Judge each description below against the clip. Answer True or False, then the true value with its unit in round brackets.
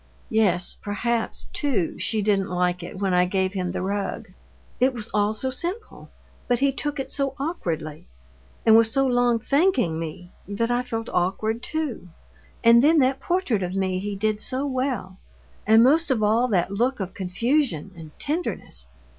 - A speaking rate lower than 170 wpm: False (175 wpm)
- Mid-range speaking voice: False (220 Hz)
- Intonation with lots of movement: True (5.7 semitones)